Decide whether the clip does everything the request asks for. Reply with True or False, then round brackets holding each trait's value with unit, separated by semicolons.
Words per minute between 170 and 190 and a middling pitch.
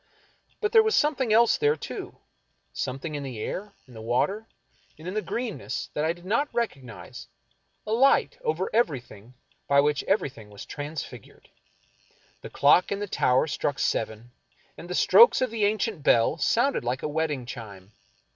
True (175 wpm; 160 Hz)